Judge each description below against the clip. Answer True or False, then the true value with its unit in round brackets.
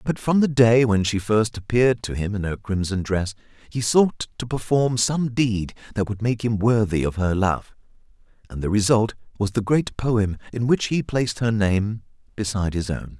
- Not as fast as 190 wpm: False (200 wpm)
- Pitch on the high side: False (110 Hz)